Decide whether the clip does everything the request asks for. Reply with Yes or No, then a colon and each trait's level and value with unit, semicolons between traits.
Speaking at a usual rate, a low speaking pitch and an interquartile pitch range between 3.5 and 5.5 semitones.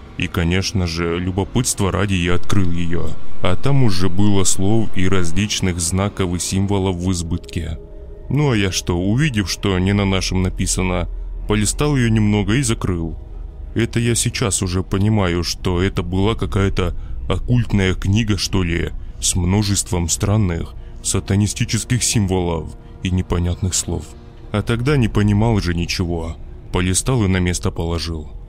No: average, 140 wpm; very low, 95 Hz; average, 3.1 semitones